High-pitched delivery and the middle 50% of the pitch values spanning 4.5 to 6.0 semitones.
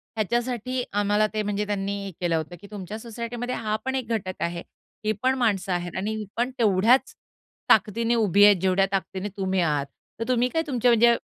No: high, 210 Hz; average, 3.7 semitones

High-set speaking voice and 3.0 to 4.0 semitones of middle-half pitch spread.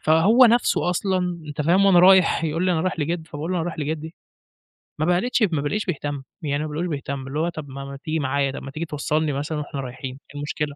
No: medium, 155 Hz; average, 3.5 semitones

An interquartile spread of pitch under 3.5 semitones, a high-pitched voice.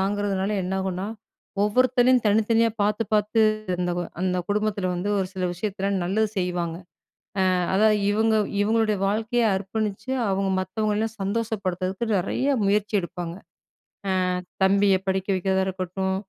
Yes: narrow, 2.5 semitones; high, 200 Hz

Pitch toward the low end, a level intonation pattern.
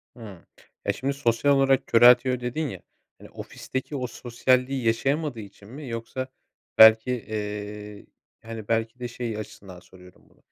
No: low, 115 Hz; average, 3.2 semitones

